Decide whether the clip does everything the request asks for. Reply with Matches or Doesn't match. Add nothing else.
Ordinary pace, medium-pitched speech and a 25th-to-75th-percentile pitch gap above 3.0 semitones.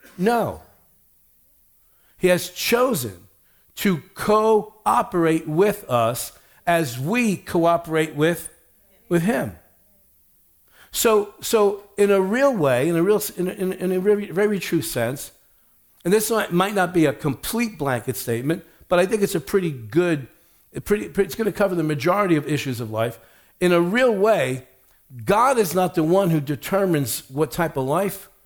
Matches